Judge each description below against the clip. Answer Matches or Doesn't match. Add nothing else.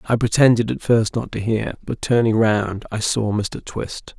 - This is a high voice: Doesn't match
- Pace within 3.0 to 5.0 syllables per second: Matches